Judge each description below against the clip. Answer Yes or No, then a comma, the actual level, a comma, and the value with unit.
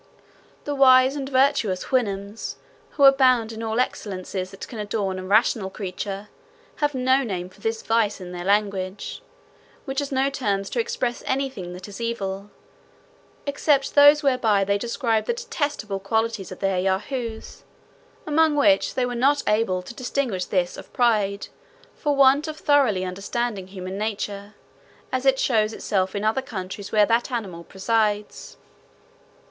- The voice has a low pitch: No, high, 220 Hz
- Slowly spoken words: No, average, 155 wpm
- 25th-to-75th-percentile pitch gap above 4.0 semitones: Yes, average, 5.0 semitones